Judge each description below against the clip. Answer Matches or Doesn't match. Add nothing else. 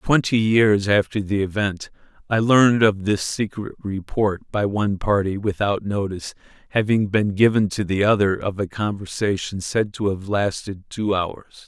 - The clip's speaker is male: Matches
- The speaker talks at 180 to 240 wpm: Doesn't match